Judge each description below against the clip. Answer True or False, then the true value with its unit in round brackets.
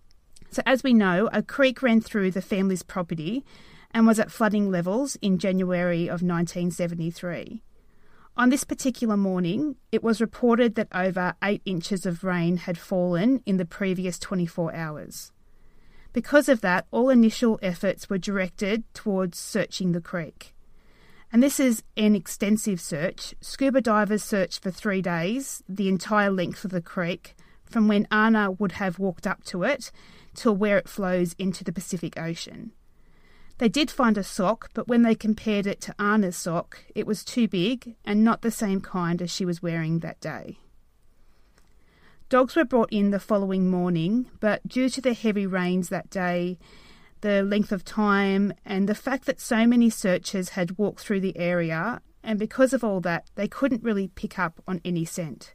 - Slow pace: False (175 wpm)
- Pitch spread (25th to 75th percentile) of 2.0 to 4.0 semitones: True (3.7 semitones)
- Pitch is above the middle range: True (200 Hz)